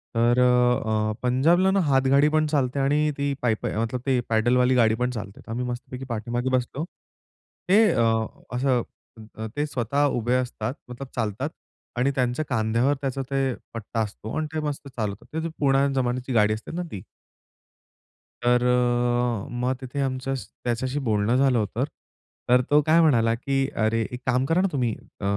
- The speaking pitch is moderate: No, low, 125 Hz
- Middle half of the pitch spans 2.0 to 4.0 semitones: Yes, average, 2.9 semitones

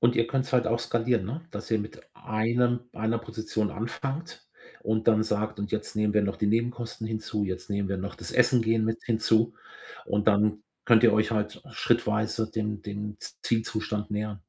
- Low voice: Yes, low, 110 Hz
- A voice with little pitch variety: Yes, narrow, 1.7 semitones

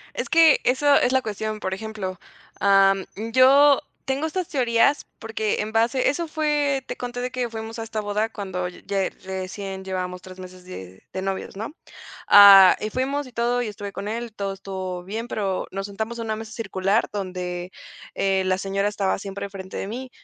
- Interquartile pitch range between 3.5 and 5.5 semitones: Yes, average, 4.0 semitones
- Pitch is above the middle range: Yes, high, 210 Hz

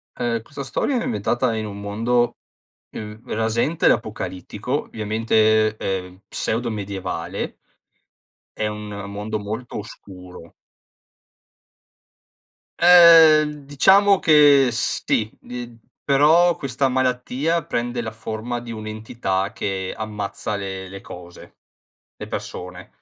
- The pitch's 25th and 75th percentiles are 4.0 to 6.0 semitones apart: Yes, average, 4.5 semitones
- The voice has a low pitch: Yes, low, 110 Hz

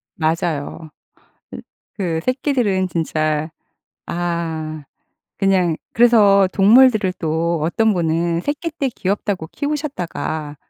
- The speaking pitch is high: No, medium, 175 Hz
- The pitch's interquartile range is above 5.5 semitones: No, average, 5.2 semitones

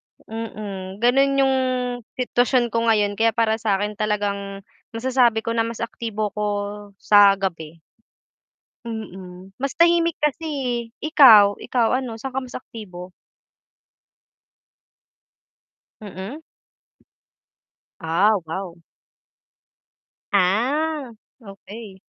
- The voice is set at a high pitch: Yes, high, 220 Hz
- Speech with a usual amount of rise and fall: Yes, average, 4.0 semitones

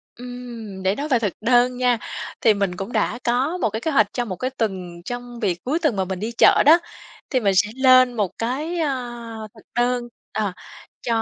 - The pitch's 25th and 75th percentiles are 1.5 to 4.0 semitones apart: Yes, average, 3.3 semitones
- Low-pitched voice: No, high, 235 Hz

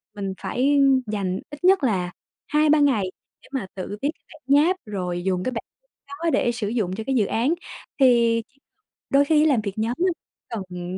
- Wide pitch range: Yes, wide, 6.5 semitones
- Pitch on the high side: Yes, high, 235 Hz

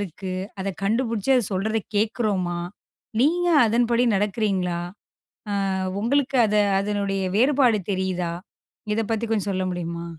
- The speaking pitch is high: Yes, high, 210 Hz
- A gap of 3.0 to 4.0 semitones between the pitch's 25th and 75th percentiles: Yes, average, 3.6 semitones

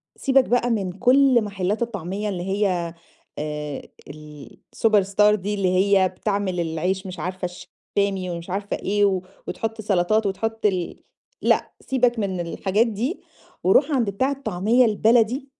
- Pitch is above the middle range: Yes, high, 200 Hz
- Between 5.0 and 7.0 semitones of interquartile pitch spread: No, average, 3.5 semitones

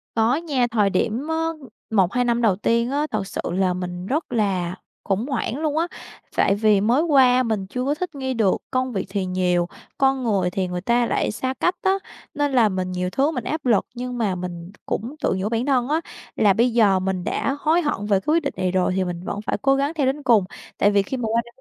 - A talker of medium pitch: No, high, 230 Hz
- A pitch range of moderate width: No, wide, 5.8 semitones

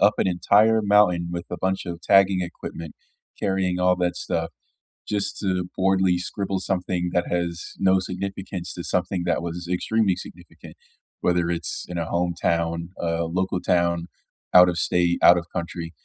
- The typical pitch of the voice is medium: No, very low, 90 Hz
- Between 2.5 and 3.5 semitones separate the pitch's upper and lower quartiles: No, narrow, 1.6 semitones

